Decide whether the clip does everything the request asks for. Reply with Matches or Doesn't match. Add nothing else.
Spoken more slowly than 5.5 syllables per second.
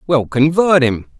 Matches